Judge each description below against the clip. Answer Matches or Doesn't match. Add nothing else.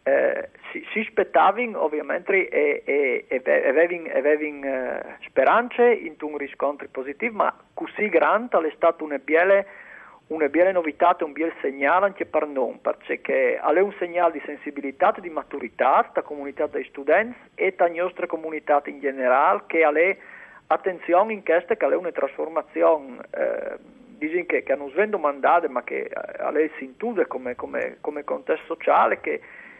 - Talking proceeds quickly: Doesn't match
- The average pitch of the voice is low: Doesn't match